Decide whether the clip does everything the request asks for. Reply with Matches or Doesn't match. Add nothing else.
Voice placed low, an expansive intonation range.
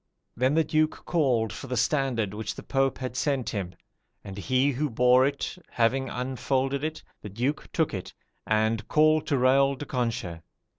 Doesn't match